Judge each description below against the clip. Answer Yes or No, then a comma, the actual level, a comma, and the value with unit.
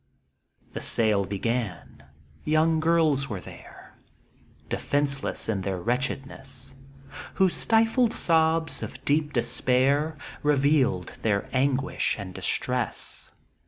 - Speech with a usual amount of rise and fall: No, wide, 5.8 semitones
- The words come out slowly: Yes, slow, 100 wpm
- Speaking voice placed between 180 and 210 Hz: No, low, 135 Hz